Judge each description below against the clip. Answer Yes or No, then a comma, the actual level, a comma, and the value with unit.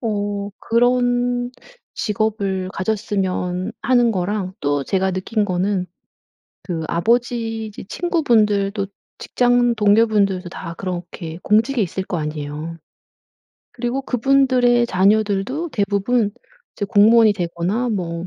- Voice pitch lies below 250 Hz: Yes, high, 205 Hz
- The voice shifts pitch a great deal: No, average, 4.3 semitones